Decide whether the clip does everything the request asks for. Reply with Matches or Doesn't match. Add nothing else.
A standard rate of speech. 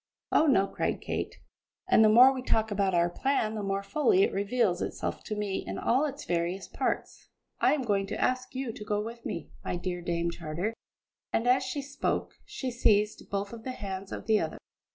Doesn't match